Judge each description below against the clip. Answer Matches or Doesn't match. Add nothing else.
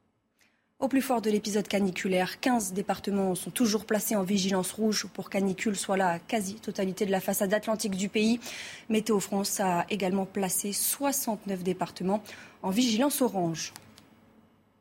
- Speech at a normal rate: Doesn't match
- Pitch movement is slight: Matches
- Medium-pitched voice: Doesn't match